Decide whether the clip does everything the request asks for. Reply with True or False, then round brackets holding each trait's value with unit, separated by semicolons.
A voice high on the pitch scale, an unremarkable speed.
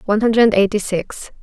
True (210 Hz; 170 wpm)